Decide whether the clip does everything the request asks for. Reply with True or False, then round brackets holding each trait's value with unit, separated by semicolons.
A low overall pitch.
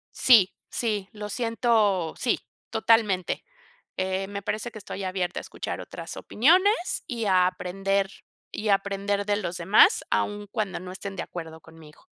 False (200 Hz)